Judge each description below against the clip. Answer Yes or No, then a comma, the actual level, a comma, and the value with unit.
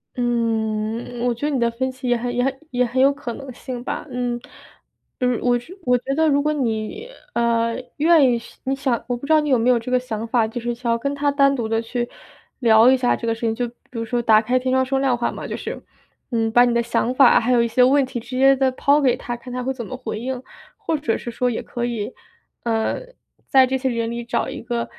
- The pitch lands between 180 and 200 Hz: No, high, 245 Hz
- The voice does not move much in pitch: Yes, narrow, 2.1 semitones